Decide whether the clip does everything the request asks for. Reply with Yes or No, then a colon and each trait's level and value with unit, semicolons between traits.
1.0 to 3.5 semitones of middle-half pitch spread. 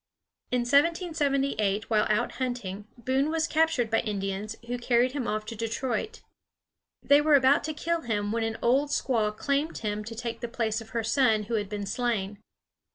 No: average, 4.5 semitones